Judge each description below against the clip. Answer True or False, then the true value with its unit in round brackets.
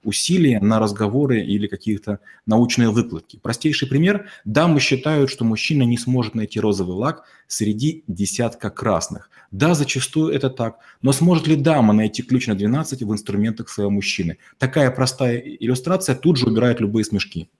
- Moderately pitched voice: False (120 Hz)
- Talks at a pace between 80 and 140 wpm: False (155 wpm)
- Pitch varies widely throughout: False (4.5 semitones)